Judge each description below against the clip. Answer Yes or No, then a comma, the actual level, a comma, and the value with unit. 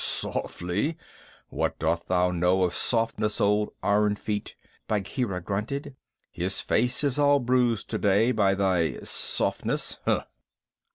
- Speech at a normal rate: No, slow, 115 wpm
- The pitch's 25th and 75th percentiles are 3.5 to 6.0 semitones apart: Yes, average, 4.8 semitones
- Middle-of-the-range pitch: No, low, 105 Hz